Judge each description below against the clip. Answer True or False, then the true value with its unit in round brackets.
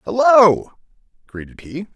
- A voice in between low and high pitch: True (165 Hz)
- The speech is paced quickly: False (90 wpm)